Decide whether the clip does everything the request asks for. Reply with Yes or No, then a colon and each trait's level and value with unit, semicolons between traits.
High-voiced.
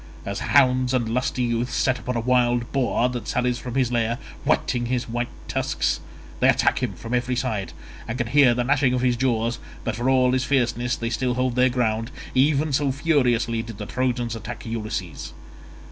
No: low, 125 Hz